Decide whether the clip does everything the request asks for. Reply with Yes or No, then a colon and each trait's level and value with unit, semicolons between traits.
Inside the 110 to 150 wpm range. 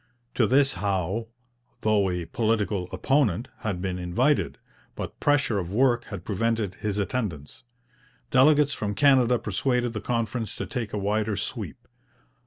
Yes: average, 140 wpm